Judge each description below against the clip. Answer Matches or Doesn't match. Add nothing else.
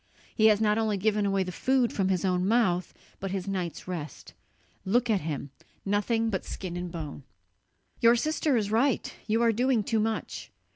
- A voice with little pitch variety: Doesn't match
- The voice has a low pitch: Doesn't match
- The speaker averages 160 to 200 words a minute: Matches